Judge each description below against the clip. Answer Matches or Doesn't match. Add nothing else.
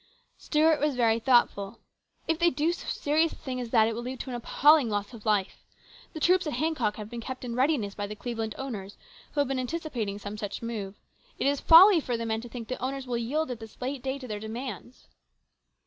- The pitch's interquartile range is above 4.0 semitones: Matches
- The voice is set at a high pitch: Matches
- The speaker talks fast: Matches